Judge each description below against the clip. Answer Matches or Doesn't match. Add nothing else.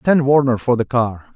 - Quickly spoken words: Matches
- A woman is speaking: Doesn't match